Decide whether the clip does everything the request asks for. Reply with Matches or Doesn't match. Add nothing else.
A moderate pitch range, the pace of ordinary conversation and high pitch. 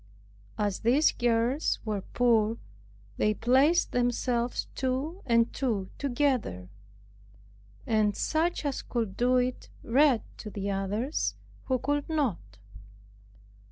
Doesn't match